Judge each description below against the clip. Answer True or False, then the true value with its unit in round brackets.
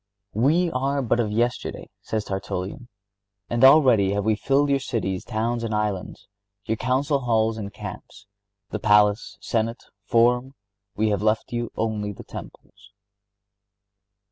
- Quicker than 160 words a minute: False (140 wpm)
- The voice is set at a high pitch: False (115 Hz)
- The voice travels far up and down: False (3.4 semitones)